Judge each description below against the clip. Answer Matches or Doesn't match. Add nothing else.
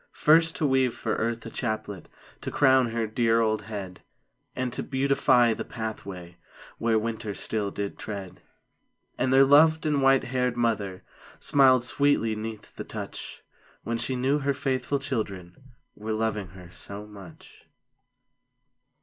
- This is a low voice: Matches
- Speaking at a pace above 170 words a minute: Doesn't match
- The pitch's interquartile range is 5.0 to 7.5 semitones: Doesn't match